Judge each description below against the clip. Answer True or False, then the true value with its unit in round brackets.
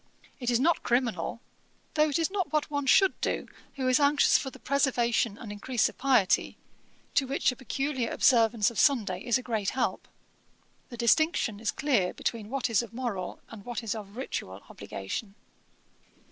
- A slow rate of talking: False (175 wpm)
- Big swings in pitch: False (4.0 semitones)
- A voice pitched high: True (245 Hz)